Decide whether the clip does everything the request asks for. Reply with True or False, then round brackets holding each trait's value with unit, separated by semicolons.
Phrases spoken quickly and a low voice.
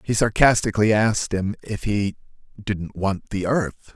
False (150 wpm; 100 Hz)